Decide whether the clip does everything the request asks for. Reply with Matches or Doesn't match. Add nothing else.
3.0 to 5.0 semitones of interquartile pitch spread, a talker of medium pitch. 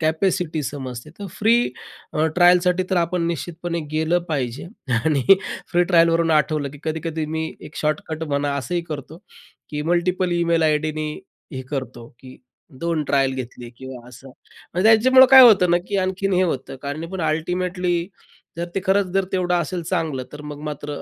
Matches